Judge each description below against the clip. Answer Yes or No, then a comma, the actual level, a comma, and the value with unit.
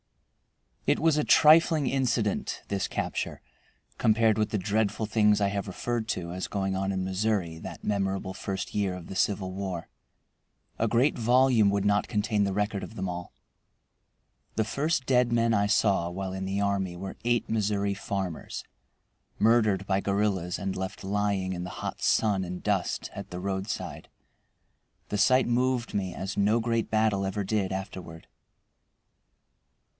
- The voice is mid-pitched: No, low, 100 Hz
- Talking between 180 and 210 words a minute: No, average, 160 wpm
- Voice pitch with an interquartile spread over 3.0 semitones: No, average, 2.7 semitones